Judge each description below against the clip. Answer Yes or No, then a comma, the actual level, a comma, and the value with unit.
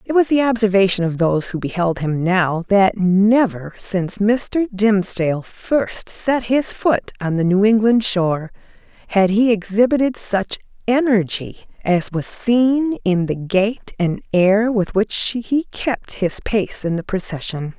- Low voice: No, high, 205 Hz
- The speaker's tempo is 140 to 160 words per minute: Yes, average, 155 wpm